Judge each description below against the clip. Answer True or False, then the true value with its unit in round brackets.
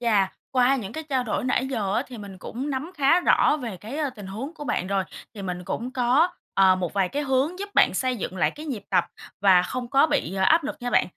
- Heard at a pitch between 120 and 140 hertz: False (245 Hz)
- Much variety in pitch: True (5.9 semitones)